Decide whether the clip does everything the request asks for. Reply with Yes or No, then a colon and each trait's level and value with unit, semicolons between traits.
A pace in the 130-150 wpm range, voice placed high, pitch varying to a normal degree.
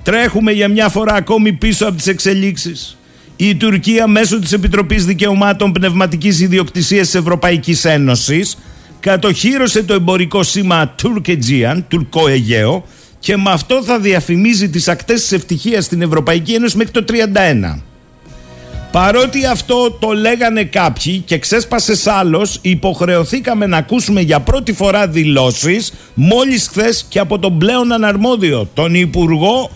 Yes: average, 135 wpm; high, 195 Hz; average, 4.2 semitones